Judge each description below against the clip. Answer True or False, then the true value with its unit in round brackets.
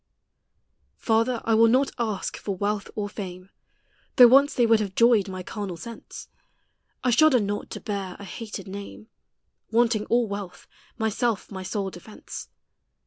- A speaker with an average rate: True (150 wpm)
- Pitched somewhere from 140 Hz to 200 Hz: False (215 Hz)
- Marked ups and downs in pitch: False (2.8 semitones)